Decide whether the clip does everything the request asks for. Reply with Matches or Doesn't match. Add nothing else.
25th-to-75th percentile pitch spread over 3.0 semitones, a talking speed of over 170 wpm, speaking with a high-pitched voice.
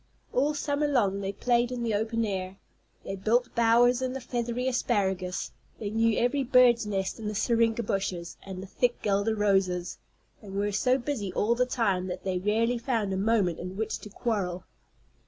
Matches